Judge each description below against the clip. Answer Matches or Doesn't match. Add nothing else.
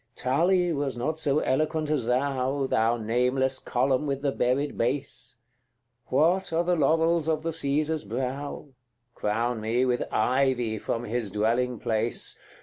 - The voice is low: Matches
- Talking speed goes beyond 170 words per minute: Doesn't match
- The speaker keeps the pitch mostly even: Doesn't match